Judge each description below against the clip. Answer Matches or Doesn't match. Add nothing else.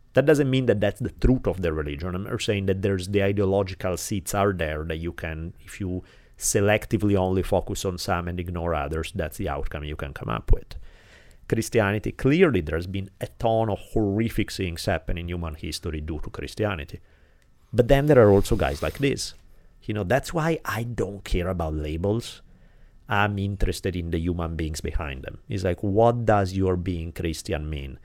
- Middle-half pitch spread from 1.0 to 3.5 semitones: Doesn't match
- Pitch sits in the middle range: Doesn't match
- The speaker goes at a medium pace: Matches